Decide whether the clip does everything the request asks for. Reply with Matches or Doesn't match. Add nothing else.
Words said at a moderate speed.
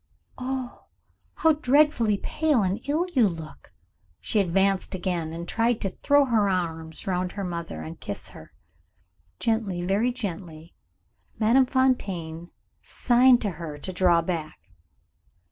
Doesn't match